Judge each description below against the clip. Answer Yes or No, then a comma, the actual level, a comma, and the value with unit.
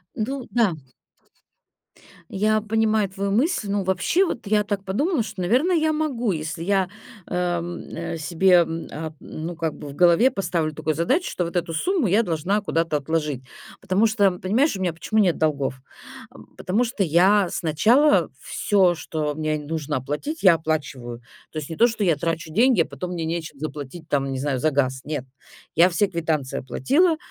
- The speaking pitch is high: No, medium, 175 Hz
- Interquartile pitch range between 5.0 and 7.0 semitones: Yes, average, 5.3 semitones